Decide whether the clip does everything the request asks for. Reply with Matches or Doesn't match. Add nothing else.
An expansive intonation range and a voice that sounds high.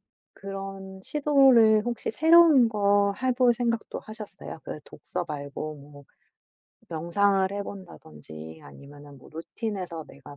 Matches